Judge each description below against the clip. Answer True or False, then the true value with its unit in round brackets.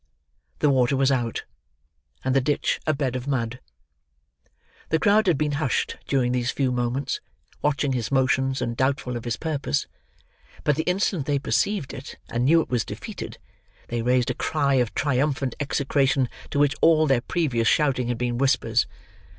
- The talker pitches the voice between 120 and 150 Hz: True (135 Hz)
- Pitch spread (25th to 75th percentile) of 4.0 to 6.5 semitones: False (2.9 semitones)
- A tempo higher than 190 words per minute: False (170 wpm)